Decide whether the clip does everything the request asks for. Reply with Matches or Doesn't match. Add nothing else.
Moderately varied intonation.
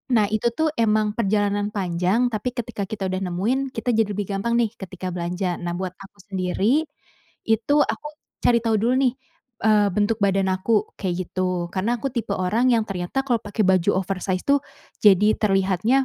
Matches